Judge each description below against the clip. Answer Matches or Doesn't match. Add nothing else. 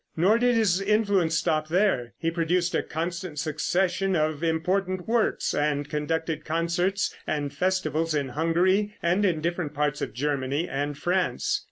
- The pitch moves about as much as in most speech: Matches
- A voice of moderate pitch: Matches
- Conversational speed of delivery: Matches